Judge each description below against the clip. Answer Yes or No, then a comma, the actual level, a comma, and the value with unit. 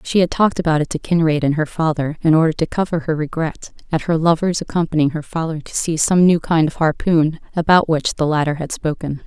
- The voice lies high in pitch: No, medium, 160 Hz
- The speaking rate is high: Yes, fast, 225 wpm